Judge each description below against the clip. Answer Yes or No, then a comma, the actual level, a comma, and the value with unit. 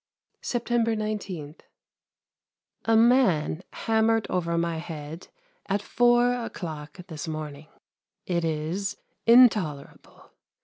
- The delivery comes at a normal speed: No, slow, 90 wpm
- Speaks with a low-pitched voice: No, medium, 185 Hz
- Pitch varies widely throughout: Yes, wide, 6.2 semitones